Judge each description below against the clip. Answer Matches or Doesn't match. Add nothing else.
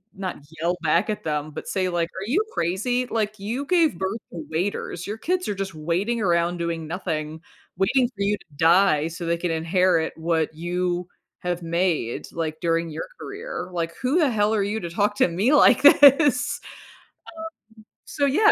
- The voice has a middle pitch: Matches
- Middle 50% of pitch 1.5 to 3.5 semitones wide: Doesn't match